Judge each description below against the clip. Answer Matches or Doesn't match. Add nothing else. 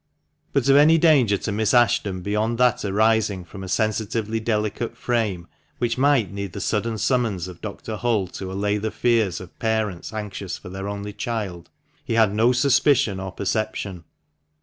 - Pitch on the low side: Matches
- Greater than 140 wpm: Matches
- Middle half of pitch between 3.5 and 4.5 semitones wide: Doesn't match